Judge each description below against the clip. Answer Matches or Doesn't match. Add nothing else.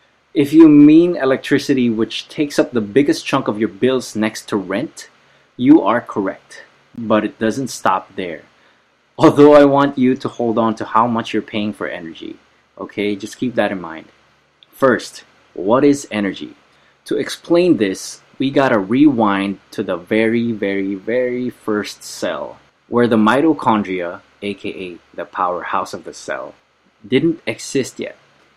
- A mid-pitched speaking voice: Doesn't match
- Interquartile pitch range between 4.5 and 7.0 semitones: Matches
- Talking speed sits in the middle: Matches